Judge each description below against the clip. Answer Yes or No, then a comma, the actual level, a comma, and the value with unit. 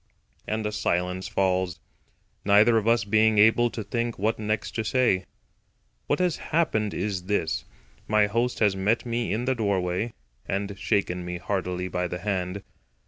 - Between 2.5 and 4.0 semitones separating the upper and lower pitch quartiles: Yes, average, 3.3 semitones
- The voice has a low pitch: Yes, low, 105 Hz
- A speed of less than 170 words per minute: Yes, average, 160 wpm